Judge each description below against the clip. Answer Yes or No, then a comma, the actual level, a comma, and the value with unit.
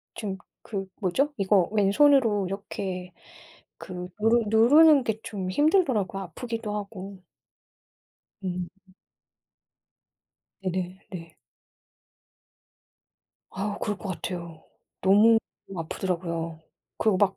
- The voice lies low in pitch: No, high, 195 Hz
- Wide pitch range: No, average, 3.3 semitones